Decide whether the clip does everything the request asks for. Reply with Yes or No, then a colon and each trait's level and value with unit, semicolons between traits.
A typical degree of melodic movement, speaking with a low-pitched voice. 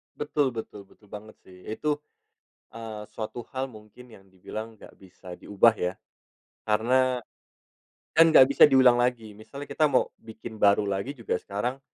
Yes: average, 3.7 semitones; low, 115 Hz